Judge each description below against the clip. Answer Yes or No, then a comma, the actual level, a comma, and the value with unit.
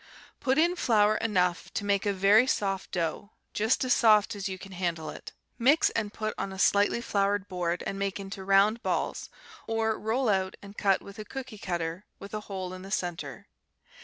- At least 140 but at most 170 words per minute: No, average, 195 wpm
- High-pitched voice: Yes, high, 200 Hz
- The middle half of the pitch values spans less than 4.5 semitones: Yes, narrow, 2.5 semitones